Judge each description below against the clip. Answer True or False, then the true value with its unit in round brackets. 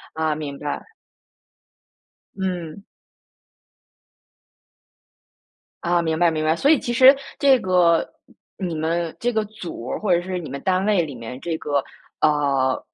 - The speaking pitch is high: False (170 Hz)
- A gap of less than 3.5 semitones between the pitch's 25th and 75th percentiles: False (3.8 semitones)